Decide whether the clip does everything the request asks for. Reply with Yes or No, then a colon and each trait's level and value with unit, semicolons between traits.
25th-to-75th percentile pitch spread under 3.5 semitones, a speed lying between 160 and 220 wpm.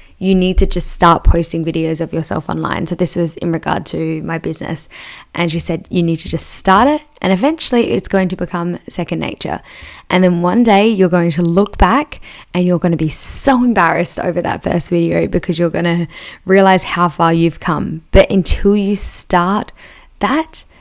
Yes: narrow, 2.4 semitones; average, 200 wpm